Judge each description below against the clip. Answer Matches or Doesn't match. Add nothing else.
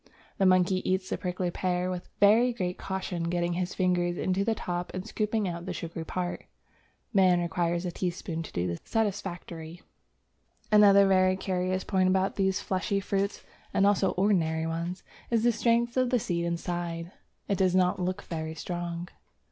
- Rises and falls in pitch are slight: Matches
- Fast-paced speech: Doesn't match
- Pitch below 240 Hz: Matches